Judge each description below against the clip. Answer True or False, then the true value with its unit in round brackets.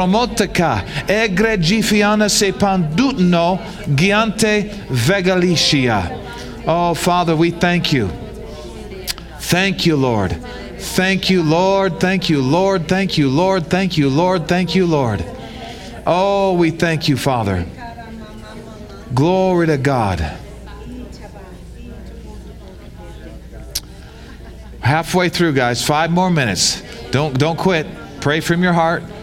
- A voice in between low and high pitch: True (170 Hz)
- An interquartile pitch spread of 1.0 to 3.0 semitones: False (5.2 semitones)